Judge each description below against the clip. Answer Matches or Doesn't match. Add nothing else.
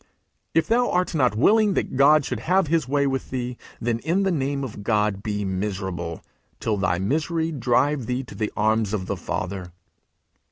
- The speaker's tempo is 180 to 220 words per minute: Matches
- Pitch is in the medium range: Doesn't match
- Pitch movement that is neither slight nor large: Doesn't match